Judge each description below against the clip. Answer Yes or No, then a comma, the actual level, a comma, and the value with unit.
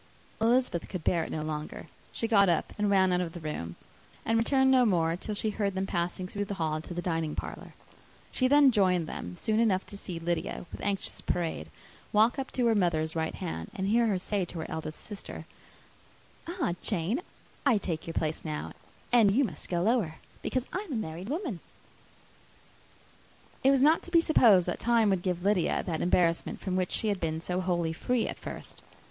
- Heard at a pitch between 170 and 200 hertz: Yes, high, 190 Hz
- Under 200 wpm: No, fast, 205 wpm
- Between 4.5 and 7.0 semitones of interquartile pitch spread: Yes, average, 5.3 semitones